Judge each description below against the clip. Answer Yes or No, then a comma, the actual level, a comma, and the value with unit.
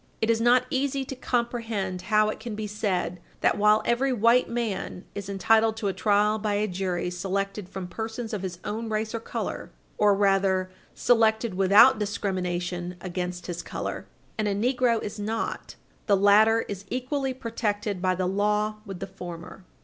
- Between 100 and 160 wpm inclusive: No, average, 170 wpm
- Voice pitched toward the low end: No, high, 210 Hz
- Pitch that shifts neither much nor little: Yes, average, 3.0 semitones